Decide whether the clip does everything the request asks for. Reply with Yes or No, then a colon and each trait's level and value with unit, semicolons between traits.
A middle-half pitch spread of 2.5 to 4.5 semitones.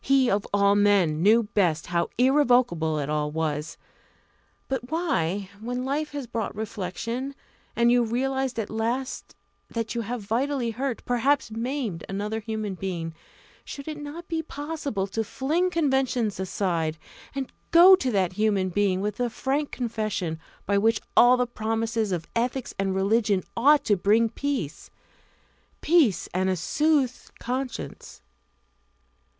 No: wide, 5.4 semitones